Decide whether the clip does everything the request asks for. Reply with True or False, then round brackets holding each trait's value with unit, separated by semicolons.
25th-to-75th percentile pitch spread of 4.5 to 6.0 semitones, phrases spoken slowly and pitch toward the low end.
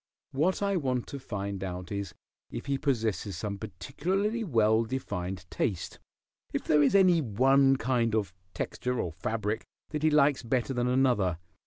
False (5.6 semitones; 160 wpm; 120 Hz)